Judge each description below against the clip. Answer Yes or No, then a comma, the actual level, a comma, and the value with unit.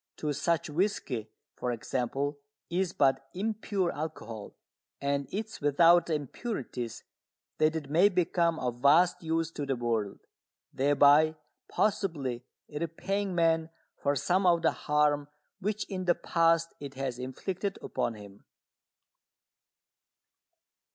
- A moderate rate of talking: No, slow, 125 wpm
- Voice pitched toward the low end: No, medium, 155 Hz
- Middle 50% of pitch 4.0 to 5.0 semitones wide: Yes, average, 4.4 semitones